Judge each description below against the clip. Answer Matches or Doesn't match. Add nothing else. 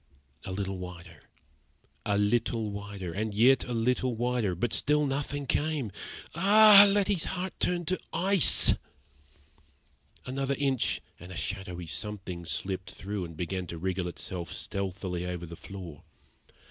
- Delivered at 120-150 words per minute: Matches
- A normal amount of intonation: Doesn't match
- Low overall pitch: Matches